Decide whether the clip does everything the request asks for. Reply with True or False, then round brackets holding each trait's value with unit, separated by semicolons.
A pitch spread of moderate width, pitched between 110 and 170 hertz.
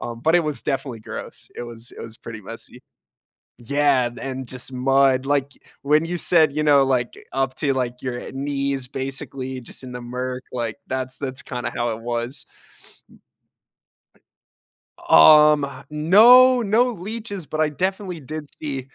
True (3.3 semitones; 135 Hz)